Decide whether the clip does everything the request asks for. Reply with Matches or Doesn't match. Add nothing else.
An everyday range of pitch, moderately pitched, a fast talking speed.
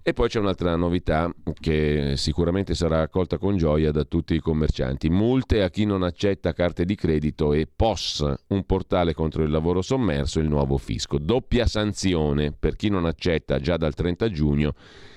Doesn't match